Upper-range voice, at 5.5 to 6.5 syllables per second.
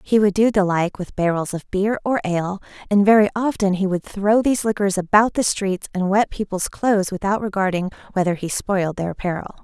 Yes: high, 195 Hz; 5.7 syllables/s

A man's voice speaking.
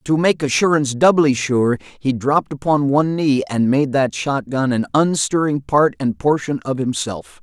Yes: male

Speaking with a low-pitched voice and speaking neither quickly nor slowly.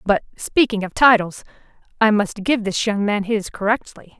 No: high, 210 Hz; average, 155 wpm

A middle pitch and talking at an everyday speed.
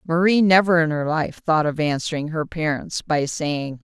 Yes: medium, 160 Hz; average, 185 wpm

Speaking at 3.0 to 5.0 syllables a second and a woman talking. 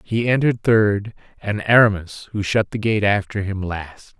No: 4.5 syllables/s; male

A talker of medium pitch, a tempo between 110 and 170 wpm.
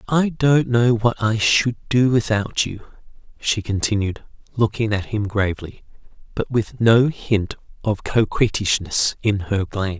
No: low, 110 Hz; average, 145 wpm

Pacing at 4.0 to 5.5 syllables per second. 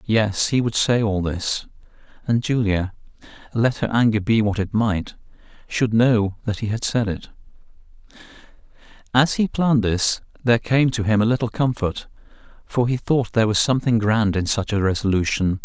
Yes: 5.0 syllables/s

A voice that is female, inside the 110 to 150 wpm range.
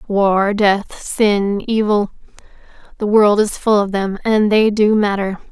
Yes: female; average, 140 wpm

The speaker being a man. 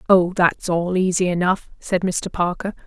No: female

